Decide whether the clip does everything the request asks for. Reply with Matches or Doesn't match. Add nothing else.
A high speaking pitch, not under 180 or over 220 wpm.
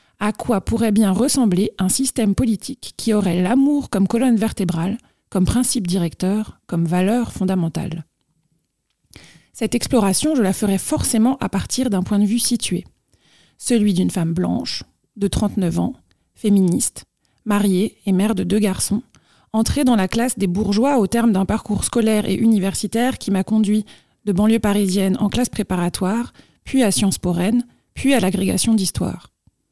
Doesn't match